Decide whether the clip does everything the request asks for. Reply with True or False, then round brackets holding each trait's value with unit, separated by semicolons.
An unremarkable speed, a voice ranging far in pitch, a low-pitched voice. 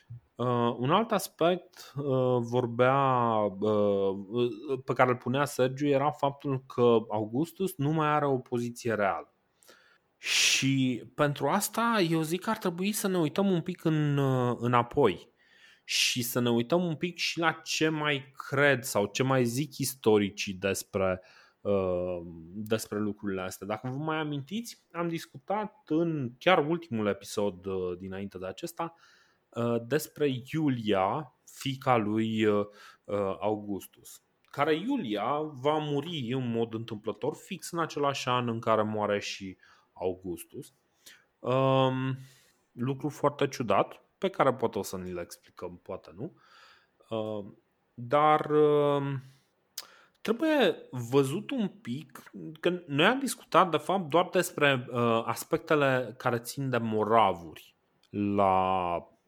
True (125 wpm; 6.0 semitones; 130 Hz)